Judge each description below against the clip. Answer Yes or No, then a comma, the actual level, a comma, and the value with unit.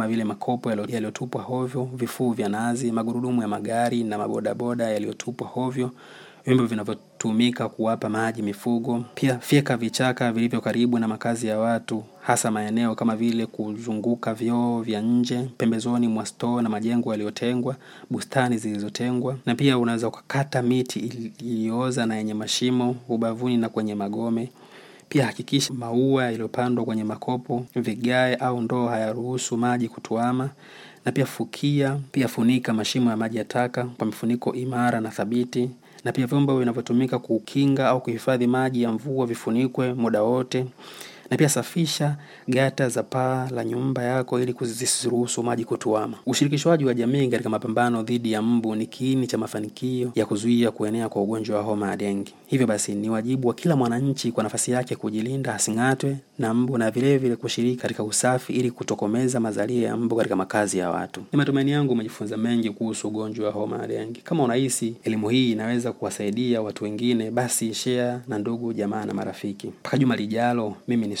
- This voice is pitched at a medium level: No, low, 120 Hz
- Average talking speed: No, fast, 155 wpm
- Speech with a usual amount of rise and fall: No, narrow, 2.2 semitones